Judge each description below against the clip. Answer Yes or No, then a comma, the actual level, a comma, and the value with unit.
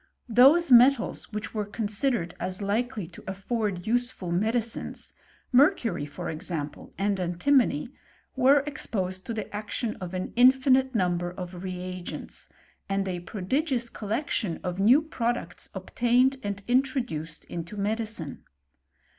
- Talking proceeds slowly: Yes, slow, 105 wpm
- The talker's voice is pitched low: No, high, 215 Hz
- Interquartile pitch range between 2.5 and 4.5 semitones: No, average, 5.3 semitones